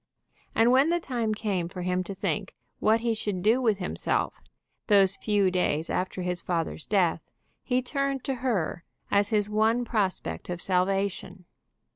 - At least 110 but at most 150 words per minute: No, average, 160 wpm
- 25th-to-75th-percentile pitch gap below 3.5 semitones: No, average, 4.0 semitones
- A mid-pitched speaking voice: No, high, 200 Hz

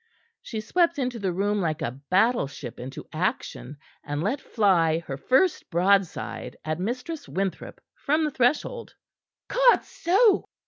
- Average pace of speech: No, slow, 130 wpm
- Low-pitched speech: No, high, 205 Hz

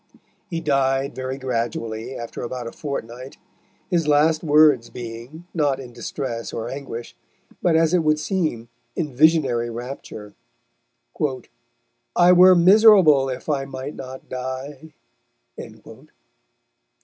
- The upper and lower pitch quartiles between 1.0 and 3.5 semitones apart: No, average, 4.2 semitones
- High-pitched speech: No, low, 135 Hz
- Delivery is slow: Yes, slow, 115 wpm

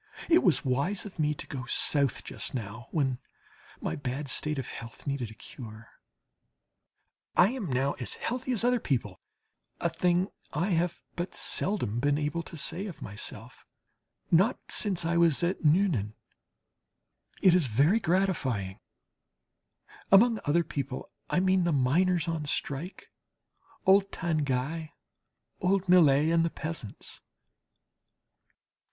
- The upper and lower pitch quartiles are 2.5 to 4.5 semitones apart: No, wide, 5.5 semitones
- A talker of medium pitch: Yes, medium, 160 Hz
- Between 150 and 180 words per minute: No, slow, 135 wpm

